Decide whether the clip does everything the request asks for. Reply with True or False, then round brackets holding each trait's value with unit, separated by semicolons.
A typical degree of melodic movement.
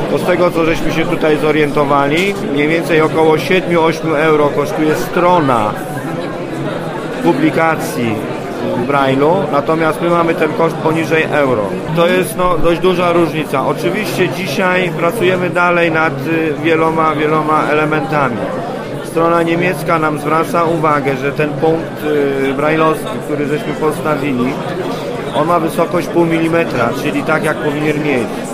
False (2.0 semitones)